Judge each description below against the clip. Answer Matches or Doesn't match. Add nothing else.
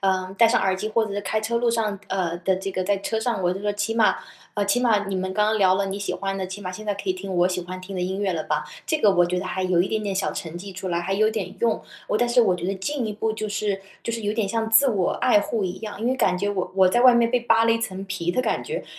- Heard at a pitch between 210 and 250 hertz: Doesn't match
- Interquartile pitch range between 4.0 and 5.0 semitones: Doesn't match